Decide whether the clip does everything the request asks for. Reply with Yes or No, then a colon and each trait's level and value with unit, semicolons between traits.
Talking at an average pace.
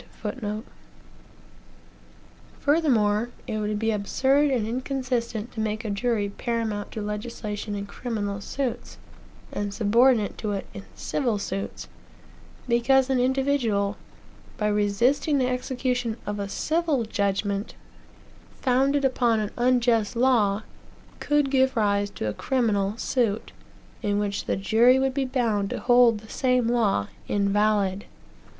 No: slow, 125 wpm